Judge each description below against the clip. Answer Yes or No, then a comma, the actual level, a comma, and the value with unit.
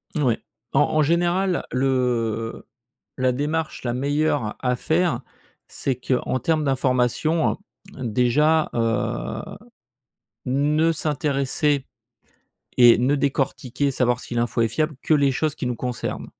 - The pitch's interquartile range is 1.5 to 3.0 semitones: No, average, 3.7 semitones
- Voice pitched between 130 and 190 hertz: Yes, low, 135 Hz